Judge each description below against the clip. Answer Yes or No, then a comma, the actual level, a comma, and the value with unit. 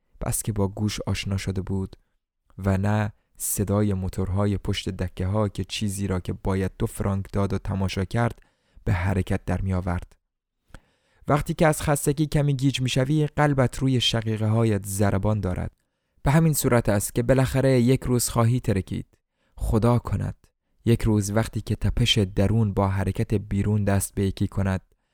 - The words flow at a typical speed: No, fast, 165 wpm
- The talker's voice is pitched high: No, low, 105 Hz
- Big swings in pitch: No, average, 3.5 semitones